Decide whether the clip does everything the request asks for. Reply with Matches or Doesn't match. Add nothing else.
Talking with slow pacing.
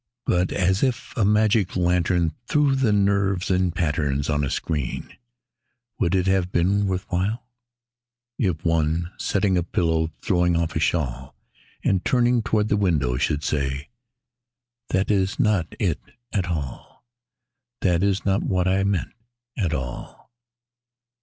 Doesn't match